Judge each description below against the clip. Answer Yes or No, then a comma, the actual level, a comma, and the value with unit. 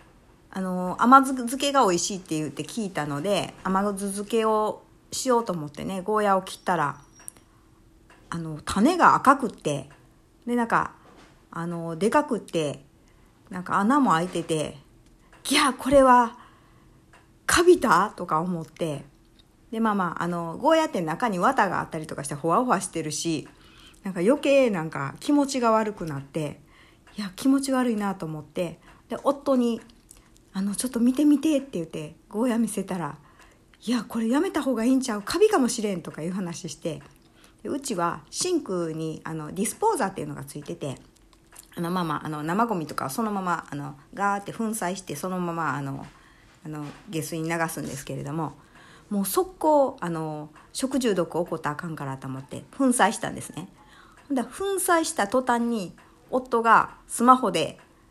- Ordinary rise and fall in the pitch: No, wide, 7.2 semitones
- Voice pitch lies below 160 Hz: No, high, 190 Hz